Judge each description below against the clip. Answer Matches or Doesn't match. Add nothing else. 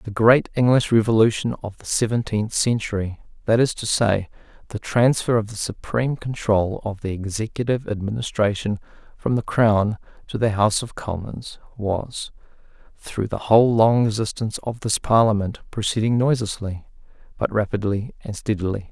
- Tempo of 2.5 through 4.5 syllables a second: Doesn't match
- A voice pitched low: Matches